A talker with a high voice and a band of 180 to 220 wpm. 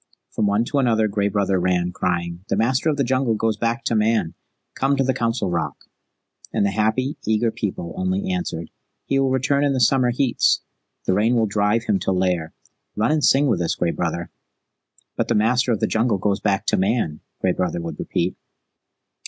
No: low, 110 Hz; average, 200 wpm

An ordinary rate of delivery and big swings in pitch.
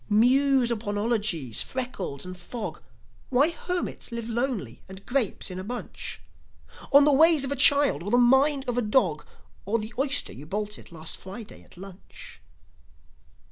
Yes: average, 160 wpm; wide, 5.8 semitones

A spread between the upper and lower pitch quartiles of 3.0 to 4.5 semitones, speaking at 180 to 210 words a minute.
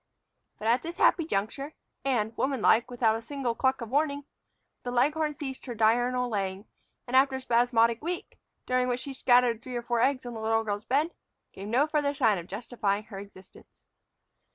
Yes: average, 3.3 semitones; average, 185 wpm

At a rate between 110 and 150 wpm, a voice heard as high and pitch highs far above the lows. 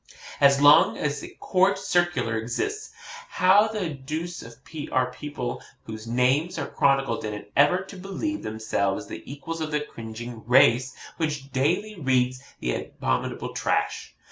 No: average, 140 wpm; medium, 140 Hz; wide, 6.1 semitones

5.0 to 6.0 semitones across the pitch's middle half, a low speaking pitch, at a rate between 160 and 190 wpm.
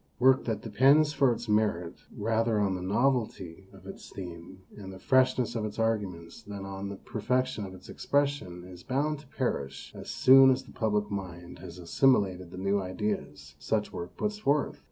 Yes: wide, 5.6 semitones; low, 105 Hz; average, 185 wpm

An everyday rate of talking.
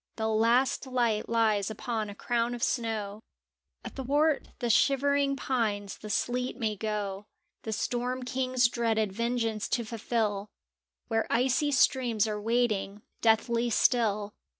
No: slow, 125 wpm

